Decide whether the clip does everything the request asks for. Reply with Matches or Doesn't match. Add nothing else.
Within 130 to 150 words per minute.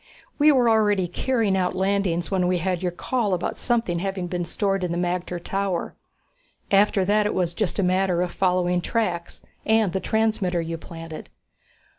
Doesn't match